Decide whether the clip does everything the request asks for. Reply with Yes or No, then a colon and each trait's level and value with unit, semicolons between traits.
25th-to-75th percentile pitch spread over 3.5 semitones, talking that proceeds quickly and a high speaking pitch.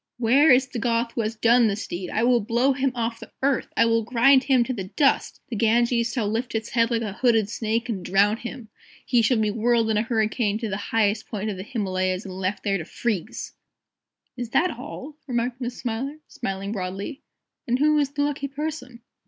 No: average, 2.9 semitones; fast, 215 wpm; high, 230 Hz